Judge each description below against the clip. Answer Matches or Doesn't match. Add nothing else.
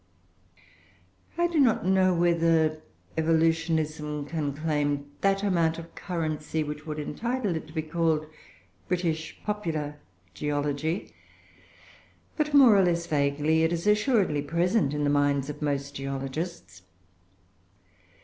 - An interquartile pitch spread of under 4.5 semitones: Matches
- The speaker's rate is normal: Doesn't match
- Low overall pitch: Doesn't match